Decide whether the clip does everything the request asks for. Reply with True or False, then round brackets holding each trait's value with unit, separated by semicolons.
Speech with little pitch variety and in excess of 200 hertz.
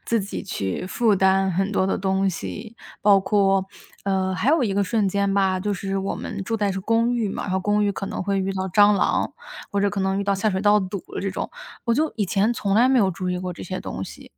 False (1.6 semitones; 195 Hz)